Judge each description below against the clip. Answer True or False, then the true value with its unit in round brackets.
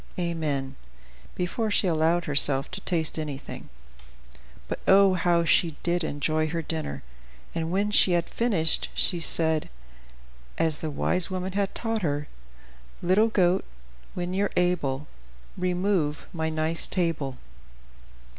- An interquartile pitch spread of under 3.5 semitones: True (2.8 semitones)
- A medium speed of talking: False (125 wpm)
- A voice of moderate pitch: True (170 Hz)